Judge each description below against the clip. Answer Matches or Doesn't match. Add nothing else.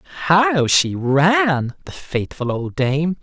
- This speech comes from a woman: Doesn't match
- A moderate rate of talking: Doesn't match